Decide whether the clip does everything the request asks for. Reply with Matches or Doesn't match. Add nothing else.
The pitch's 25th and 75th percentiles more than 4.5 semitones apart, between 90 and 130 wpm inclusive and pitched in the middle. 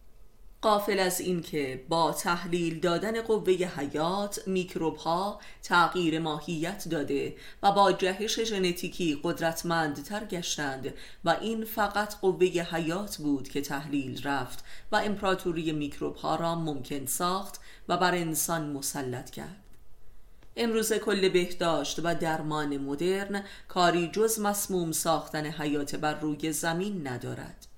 Doesn't match